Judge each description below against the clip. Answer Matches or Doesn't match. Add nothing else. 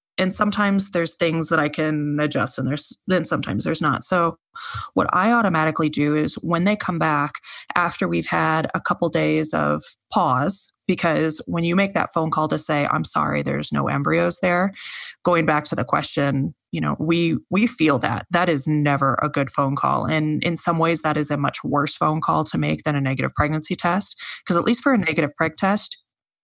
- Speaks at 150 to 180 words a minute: Doesn't match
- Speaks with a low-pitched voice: Doesn't match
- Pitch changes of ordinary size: Matches